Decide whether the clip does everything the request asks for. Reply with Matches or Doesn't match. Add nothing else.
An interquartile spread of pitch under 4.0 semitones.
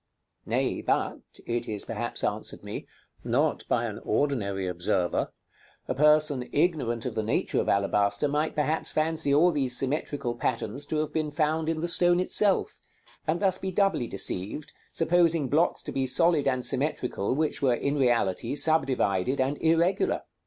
Doesn't match